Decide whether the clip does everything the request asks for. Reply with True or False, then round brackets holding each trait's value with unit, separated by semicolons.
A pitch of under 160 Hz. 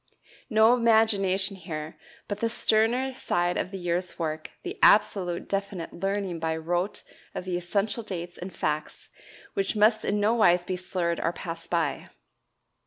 False (185 Hz)